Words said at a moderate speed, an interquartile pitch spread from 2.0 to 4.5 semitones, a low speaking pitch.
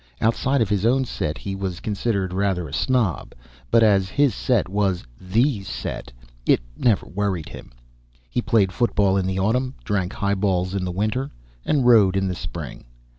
Yes: average, 175 wpm; average, 3.6 semitones; low, 100 Hz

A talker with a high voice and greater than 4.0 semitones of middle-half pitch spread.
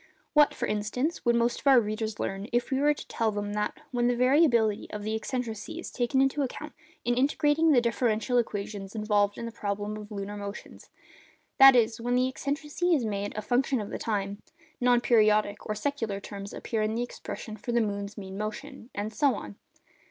No: high, 230 Hz; average, 3.7 semitones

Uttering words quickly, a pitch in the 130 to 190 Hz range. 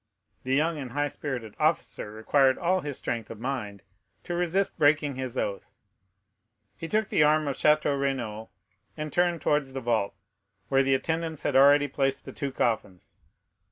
No: average, 165 wpm; medium, 140 Hz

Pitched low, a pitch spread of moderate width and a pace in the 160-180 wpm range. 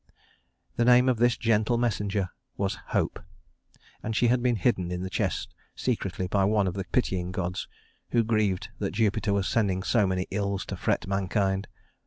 Yes: low, 100 Hz; average, 3.3 semitones; average, 175 wpm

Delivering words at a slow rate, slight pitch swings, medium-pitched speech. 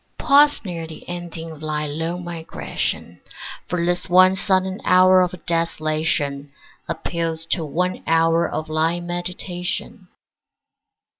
Yes: slow, 120 wpm; narrow, 2.1 semitones; medium, 170 Hz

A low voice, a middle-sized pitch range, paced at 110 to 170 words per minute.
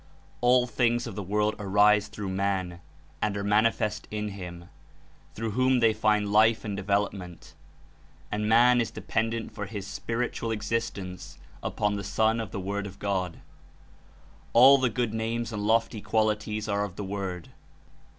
No: low, 105 Hz; narrow, 2.3 semitones; average, 160 wpm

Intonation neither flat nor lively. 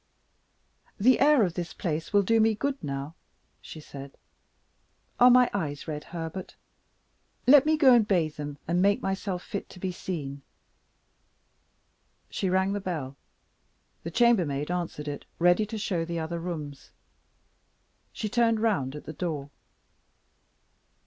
No: wide, 5.8 semitones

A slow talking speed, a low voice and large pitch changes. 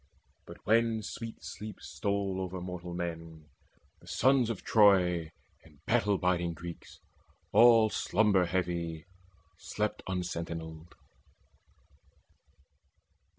No: slow, 95 wpm; very low, 90 Hz; average, 3.9 semitones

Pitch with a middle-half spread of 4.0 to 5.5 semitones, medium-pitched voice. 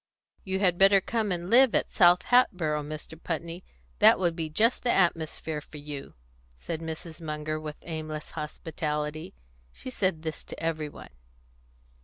No: average, 3.1 semitones; medium, 160 Hz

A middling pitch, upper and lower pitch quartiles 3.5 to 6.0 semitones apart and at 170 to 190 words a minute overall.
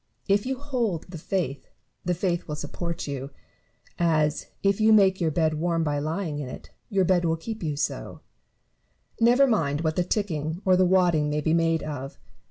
Yes: medium, 170 Hz; average, 4.0 semitones; average, 185 wpm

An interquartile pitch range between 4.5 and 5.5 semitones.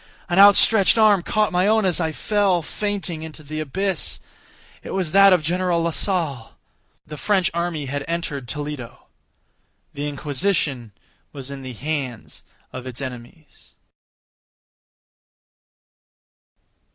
Yes: average, 5.1 semitones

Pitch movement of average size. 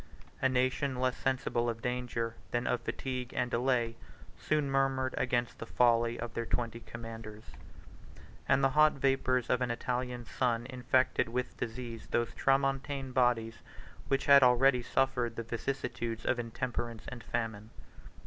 No: narrow, 2.0 semitones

